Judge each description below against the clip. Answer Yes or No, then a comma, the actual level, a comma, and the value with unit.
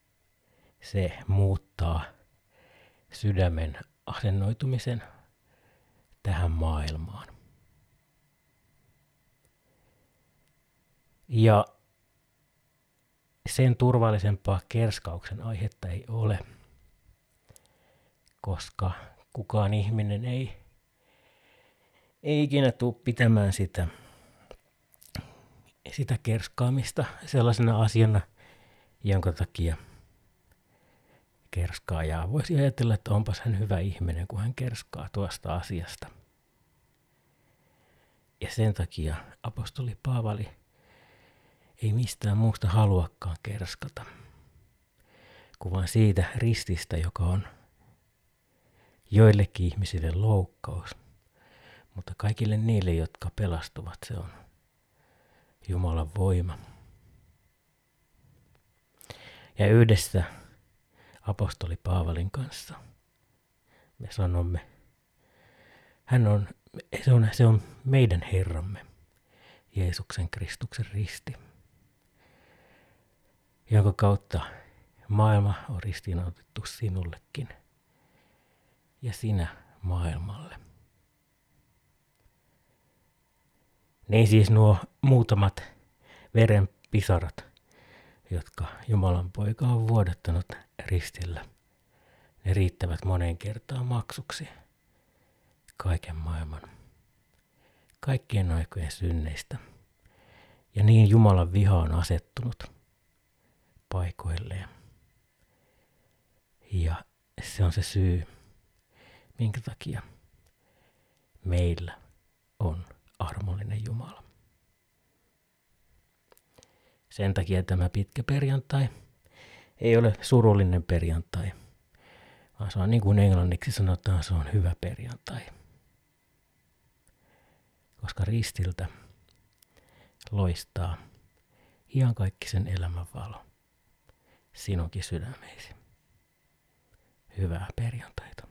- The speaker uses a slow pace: Yes, slow, 75 wpm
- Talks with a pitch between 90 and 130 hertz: Yes, low, 100 Hz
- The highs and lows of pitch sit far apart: No, average, 4.0 semitones